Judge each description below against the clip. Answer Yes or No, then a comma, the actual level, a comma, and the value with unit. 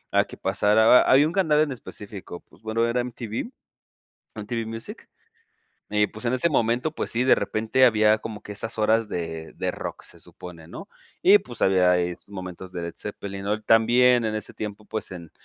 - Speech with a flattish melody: No, average, 3.4 semitones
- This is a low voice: Yes, low, 110 Hz